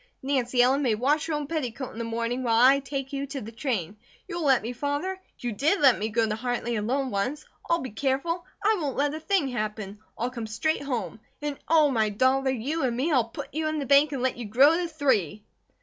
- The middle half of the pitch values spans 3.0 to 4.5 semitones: Yes, average, 4.0 semitones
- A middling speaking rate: No, fast, 235 wpm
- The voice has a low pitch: No, very high, 265 Hz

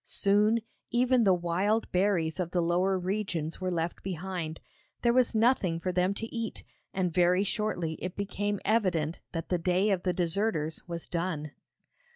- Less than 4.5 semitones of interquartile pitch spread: Yes, average, 3.2 semitones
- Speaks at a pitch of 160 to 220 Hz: Yes, medium, 185 Hz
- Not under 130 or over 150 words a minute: No, average, 165 wpm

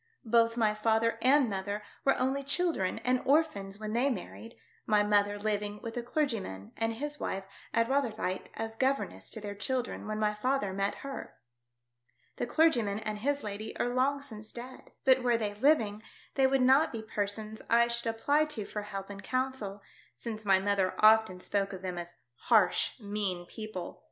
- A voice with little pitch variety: No, average, 3.9 semitones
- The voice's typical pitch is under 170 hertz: No, high, 220 Hz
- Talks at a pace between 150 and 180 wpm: Yes, average, 175 wpm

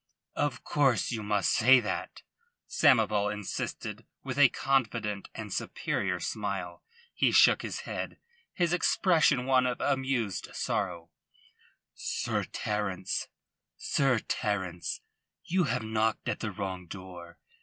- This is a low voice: Yes, low, 110 Hz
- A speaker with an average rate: No, slow, 110 wpm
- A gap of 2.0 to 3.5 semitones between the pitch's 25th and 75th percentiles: No, average, 5.2 semitones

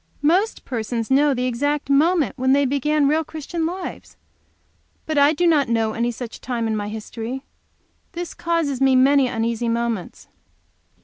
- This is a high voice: Yes, very high, 270 Hz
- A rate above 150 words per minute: Yes, average, 165 wpm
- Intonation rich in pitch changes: No, average, 4.5 semitones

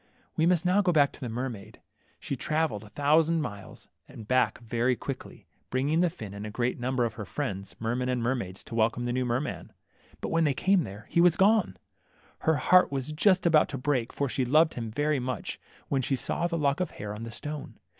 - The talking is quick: Yes, fast, 235 wpm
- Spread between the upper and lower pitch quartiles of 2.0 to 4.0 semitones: No, average, 5.1 semitones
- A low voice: Yes, low, 130 Hz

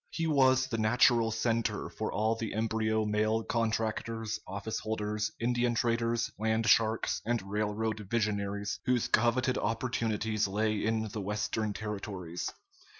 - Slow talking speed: Yes, slow, 130 wpm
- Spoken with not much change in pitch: Yes, narrow, 1.6 semitones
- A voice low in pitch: Yes, low, 110 Hz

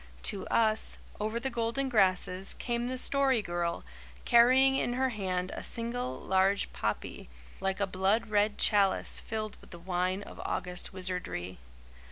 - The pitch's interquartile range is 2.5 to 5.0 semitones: Yes, average, 4.2 semitones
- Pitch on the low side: No, high, 205 Hz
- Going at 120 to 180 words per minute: Yes, average, 150 wpm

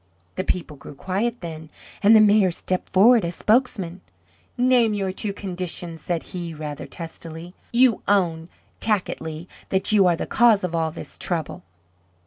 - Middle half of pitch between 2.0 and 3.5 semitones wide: No, average, 4.1 semitones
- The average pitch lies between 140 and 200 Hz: Yes, medium, 185 Hz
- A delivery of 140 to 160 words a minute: Yes, average, 155 wpm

